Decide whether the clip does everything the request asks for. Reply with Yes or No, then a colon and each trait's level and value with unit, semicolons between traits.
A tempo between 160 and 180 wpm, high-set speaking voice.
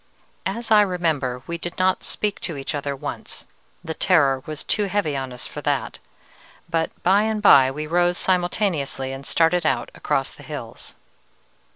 No: average, 170 wpm; medium, 165 Hz